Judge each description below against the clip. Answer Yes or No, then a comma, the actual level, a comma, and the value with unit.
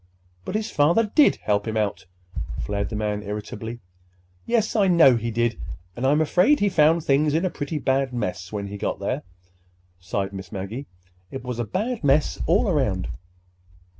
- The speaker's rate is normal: Yes, average, 170 wpm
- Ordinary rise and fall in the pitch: No, wide, 7.9 semitones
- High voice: No, low, 130 Hz